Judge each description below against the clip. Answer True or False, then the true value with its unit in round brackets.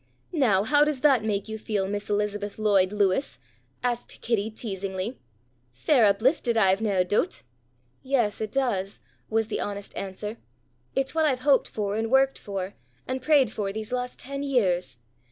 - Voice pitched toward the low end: False (220 Hz)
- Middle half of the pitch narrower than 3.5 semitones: False (4.4 semitones)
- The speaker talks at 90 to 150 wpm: False (160 wpm)